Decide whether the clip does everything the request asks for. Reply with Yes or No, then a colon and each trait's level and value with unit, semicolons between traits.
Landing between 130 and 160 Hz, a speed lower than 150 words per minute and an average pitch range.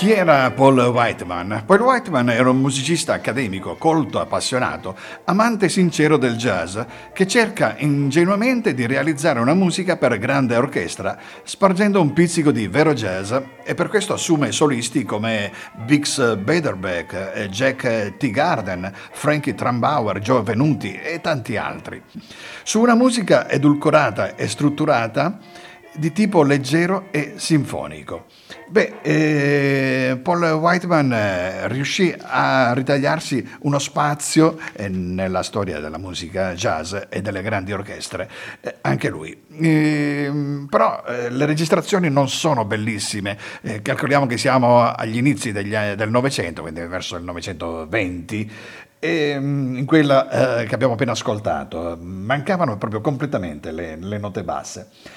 No: low, 135 Hz; average, 135 wpm; wide, 6.2 semitones